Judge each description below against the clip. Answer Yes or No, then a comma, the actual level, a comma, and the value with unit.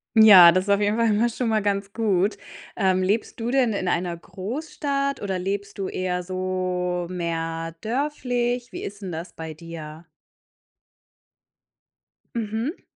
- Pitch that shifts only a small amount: No, average, 4.1 semitones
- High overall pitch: Yes, high, 195 Hz